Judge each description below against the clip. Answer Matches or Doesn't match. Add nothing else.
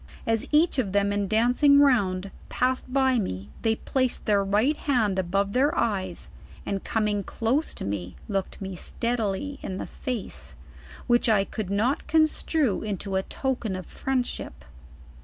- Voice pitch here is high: Matches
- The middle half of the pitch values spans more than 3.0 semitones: Matches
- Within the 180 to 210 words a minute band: Doesn't match